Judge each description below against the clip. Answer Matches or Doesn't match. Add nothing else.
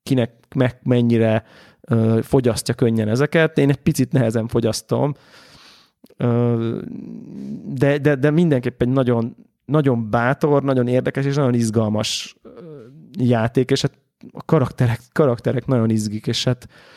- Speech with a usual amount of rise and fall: Matches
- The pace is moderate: Matches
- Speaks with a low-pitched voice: Matches